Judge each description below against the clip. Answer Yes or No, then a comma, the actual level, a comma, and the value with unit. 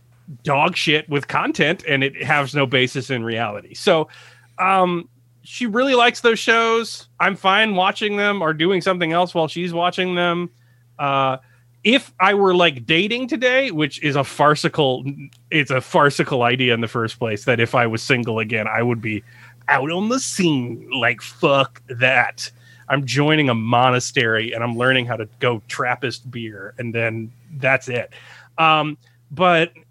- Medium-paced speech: Yes, average, 165 wpm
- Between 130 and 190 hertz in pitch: Yes, low, 135 Hz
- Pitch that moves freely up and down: Yes, wide, 6.1 semitones